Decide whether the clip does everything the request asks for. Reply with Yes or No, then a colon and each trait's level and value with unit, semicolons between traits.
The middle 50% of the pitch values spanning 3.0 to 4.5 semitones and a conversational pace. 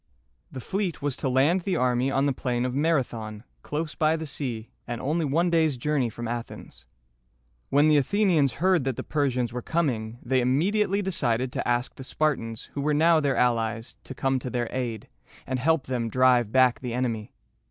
Yes: average, 4.2 semitones; average, 195 wpm